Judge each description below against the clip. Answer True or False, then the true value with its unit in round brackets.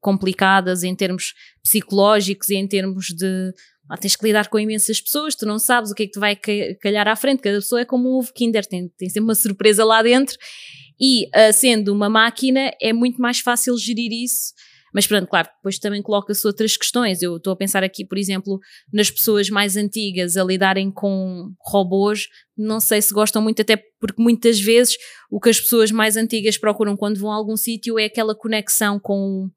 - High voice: True (210 Hz)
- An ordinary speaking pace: False (205 wpm)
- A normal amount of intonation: False (2.3 semitones)